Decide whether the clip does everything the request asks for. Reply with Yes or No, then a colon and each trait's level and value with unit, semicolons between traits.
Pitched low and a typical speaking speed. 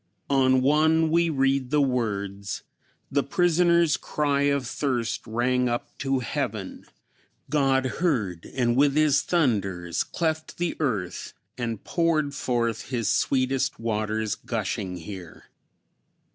No: low, 130 Hz; slow, 115 wpm